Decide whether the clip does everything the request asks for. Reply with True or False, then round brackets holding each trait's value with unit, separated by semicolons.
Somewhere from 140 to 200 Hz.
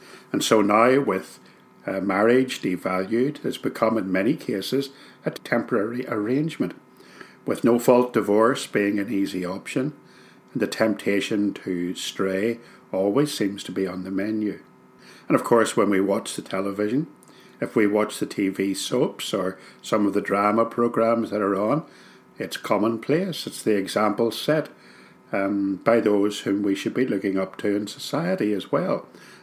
False (100 Hz)